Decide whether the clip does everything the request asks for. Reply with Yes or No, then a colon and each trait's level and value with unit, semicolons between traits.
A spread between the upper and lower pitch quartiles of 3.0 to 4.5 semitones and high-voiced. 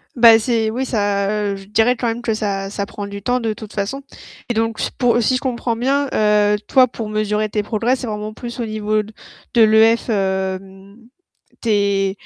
No: narrow, 2.5 semitones; high, 215 Hz